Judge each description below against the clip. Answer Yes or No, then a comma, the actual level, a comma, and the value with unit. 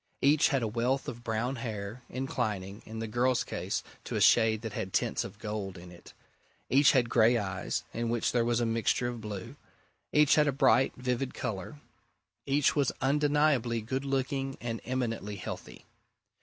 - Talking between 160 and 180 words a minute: Yes, average, 175 wpm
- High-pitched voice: No, low, 120 Hz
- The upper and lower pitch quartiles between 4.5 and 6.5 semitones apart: No, average, 3.4 semitones